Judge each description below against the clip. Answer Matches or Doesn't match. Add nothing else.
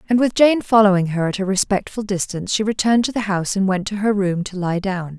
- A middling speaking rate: Doesn't match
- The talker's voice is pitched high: Matches